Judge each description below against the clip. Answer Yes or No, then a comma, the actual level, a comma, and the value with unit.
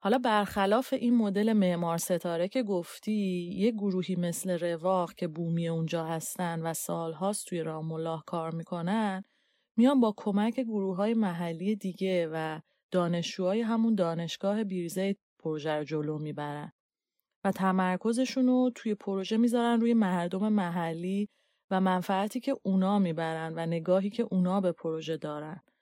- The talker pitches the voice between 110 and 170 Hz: No, medium, 185 Hz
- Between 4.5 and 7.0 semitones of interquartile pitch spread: No, average, 4.1 semitones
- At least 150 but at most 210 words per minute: No, average, 140 wpm